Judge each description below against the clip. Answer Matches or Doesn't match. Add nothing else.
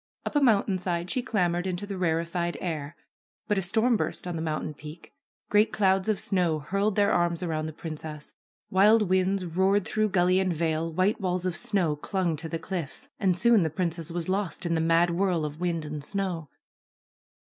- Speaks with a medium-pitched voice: Matches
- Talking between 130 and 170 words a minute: Doesn't match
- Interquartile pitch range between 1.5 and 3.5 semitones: Matches